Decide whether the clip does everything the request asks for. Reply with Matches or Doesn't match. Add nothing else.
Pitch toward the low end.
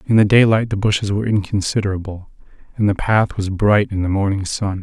Matches